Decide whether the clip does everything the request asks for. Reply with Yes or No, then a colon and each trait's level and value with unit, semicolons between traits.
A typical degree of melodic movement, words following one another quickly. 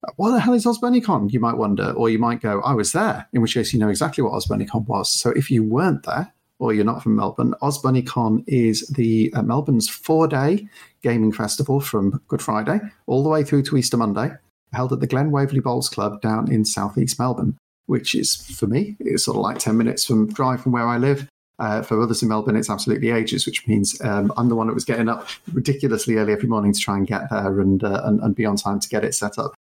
Yes: average, 4.2 semitones; fast, 240 wpm